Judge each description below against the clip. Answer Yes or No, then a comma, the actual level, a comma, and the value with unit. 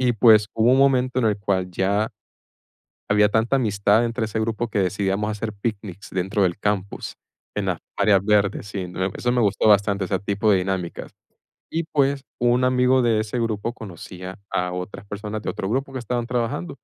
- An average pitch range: Yes, average, 3.2 semitones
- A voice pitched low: Yes, low, 105 Hz